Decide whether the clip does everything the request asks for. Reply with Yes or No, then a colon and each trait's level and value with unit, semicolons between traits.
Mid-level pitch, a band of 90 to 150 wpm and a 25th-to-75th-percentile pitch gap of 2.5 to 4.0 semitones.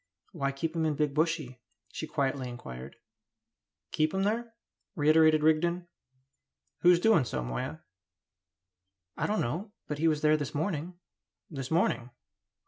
Yes: medium, 155 Hz; slow, 135 wpm; average, 3.7 semitones